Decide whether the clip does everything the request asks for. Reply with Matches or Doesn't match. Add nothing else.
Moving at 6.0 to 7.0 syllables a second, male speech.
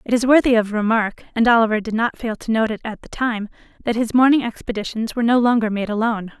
Doesn't match